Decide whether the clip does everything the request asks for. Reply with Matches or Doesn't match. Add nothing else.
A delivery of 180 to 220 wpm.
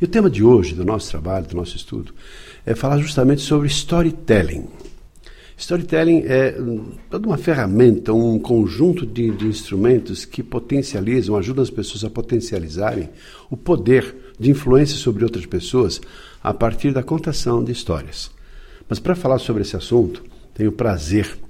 Doesn't match